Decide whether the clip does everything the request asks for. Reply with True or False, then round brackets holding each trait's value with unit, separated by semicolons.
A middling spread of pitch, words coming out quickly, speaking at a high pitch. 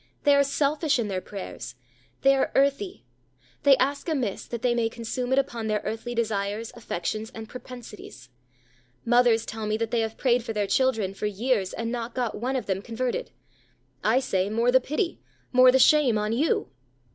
False (3.2 semitones; 185 wpm; 235 Hz)